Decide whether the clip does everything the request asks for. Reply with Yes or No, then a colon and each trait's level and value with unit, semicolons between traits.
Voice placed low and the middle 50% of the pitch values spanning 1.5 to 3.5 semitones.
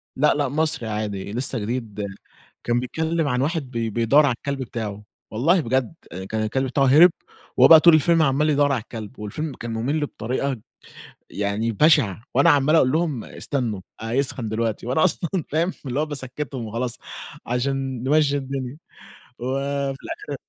No: low, 130 Hz; average, 4.2 semitones